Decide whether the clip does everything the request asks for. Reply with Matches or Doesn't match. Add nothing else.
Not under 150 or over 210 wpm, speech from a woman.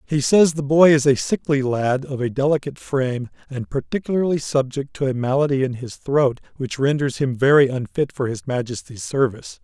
Doesn't match